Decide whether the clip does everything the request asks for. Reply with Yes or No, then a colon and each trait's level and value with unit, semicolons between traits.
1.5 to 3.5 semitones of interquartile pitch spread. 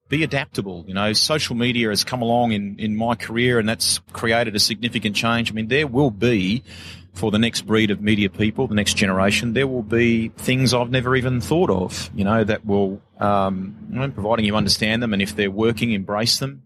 Yes: average, 2.8 semitones